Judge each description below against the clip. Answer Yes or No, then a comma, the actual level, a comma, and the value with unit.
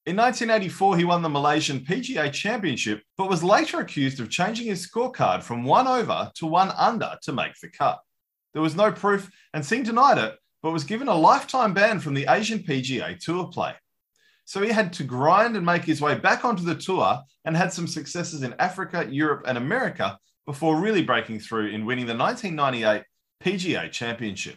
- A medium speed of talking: Yes, average, 190 wpm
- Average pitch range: No, wide, 6.5 semitones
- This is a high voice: No, medium, 170 Hz